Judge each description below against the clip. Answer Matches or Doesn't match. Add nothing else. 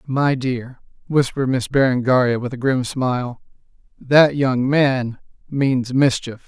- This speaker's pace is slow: Matches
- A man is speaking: Matches